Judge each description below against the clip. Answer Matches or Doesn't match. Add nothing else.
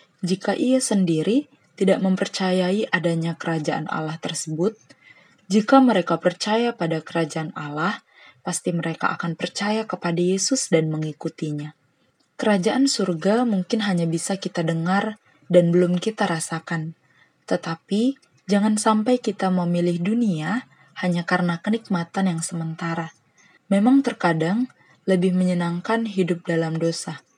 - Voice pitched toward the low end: Doesn't match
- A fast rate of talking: Doesn't match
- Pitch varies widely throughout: Doesn't match